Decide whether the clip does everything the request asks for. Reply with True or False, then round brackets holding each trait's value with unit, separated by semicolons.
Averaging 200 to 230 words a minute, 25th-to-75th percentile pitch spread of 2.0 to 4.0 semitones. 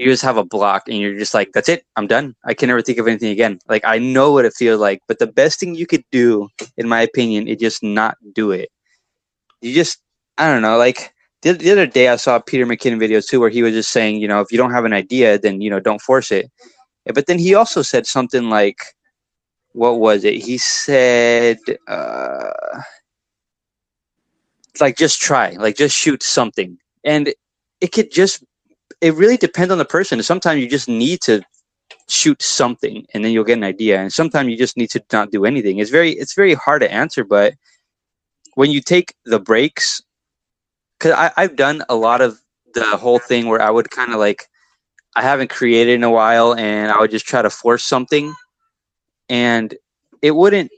False (205 wpm; 5.2 semitones)